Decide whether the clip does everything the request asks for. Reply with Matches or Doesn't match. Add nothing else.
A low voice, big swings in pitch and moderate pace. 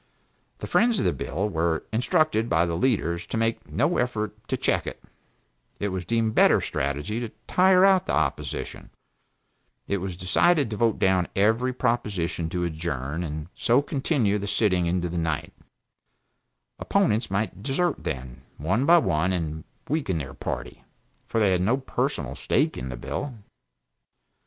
Matches